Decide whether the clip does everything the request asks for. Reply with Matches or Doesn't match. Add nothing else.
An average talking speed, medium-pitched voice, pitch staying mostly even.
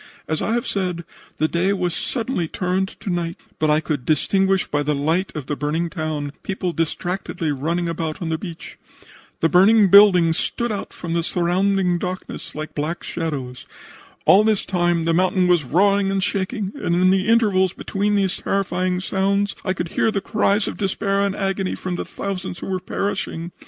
Doesn't match